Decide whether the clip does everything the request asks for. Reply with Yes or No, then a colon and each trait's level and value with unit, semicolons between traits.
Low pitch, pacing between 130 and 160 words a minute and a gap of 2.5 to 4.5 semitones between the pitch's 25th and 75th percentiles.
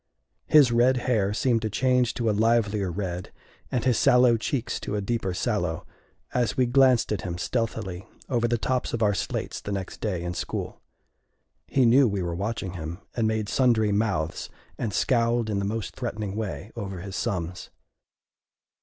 No: low, 110 Hz; average, 175 wpm; average, 3.6 semitones